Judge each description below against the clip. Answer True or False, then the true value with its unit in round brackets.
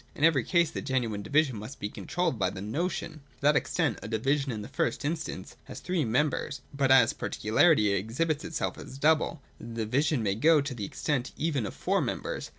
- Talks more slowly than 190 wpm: False (200 wpm)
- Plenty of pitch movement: True (5.7 semitones)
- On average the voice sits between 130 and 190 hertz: True (135 Hz)